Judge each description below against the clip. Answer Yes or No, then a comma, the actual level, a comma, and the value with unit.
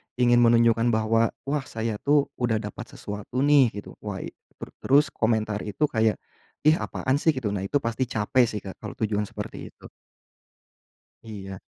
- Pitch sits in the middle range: No, low, 115 Hz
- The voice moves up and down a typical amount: Yes, average, 3.7 semitones